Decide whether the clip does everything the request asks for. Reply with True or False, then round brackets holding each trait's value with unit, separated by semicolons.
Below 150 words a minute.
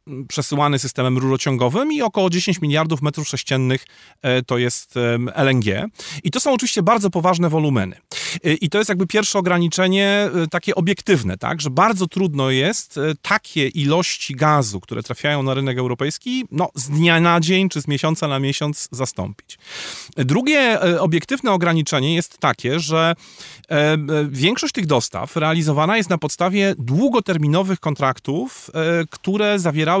True (135 wpm)